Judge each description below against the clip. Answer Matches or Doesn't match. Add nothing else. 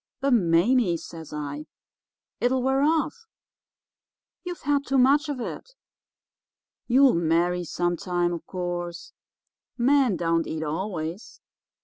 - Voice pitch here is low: Doesn't match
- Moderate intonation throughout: Doesn't match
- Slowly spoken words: Matches